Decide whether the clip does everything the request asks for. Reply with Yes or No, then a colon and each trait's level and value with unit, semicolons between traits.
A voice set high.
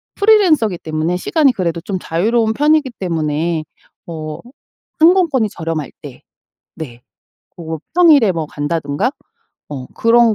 No: medium, 180 Hz